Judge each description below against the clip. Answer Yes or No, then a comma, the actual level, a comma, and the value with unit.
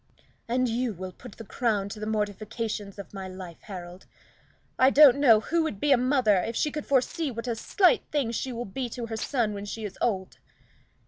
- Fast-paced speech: Yes, fast, 210 wpm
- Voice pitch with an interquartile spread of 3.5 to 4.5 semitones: Yes, average, 4.1 semitones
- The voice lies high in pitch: Yes, high, 225 Hz